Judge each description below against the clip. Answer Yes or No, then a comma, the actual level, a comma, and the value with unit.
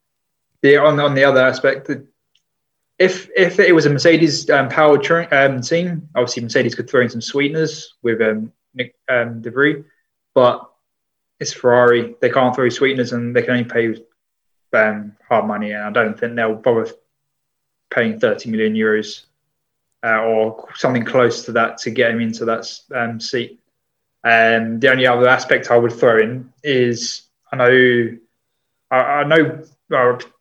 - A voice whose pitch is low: Yes, low, 125 Hz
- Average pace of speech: Yes, average, 165 wpm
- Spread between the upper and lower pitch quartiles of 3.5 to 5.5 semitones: Yes, average, 4.2 semitones